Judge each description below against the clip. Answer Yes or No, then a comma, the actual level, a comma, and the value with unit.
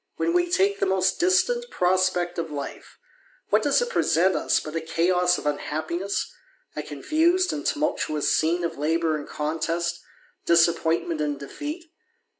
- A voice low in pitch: No, medium, 175 Hz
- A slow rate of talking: No, average, 150 wpm